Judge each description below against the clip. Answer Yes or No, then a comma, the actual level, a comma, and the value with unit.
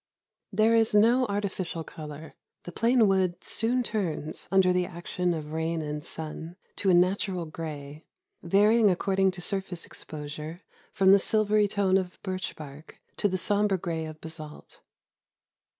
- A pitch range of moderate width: Yes, average, 4.0 semitones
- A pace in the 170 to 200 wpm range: No, average, 150 wpm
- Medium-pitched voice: Yes, medium, 180 Hz